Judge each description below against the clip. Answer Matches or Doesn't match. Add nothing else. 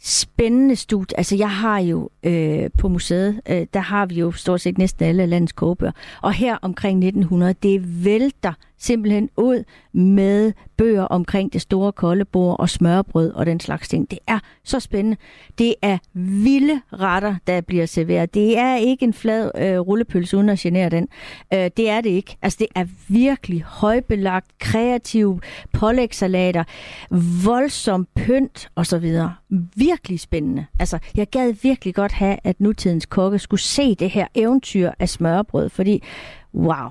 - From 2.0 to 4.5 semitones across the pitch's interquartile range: Matches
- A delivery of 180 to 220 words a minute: Doesn't match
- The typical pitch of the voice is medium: Doesn't match